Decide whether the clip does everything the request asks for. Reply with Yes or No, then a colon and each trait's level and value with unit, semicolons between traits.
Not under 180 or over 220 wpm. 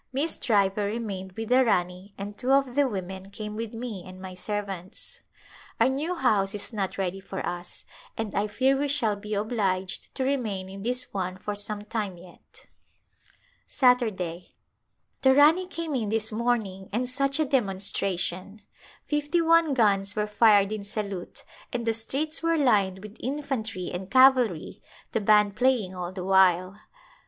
No: average, 165 wpm